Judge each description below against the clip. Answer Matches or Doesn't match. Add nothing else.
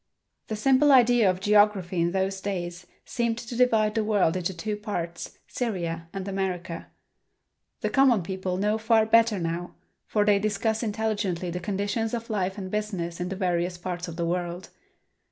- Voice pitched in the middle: Doesn't match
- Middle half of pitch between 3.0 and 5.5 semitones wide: Matches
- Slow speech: Doesn't match